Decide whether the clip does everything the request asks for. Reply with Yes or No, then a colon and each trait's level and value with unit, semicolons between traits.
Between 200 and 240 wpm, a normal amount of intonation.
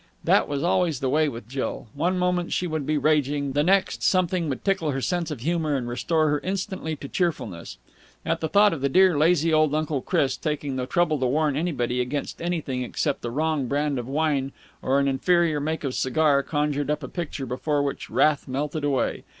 Yes: fast, 205 wpm; average, 3.3 semitones